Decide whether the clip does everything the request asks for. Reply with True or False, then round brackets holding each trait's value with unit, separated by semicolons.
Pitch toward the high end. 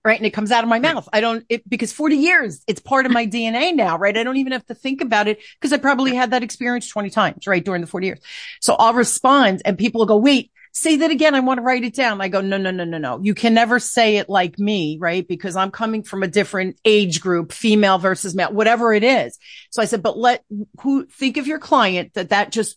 True (225 Hz)